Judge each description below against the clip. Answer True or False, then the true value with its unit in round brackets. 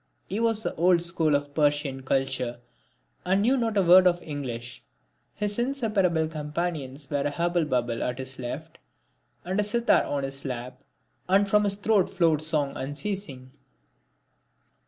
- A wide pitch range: True (6.3 semitones)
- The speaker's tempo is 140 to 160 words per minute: True (155 wpm)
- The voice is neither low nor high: True (160 Hz)